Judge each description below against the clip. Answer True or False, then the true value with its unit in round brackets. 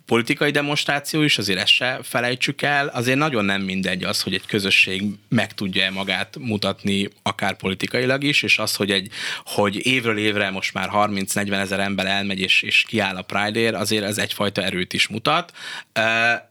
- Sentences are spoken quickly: True (175 wpm)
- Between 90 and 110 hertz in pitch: True (105 Hz)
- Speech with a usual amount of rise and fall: True (3.7 semitones)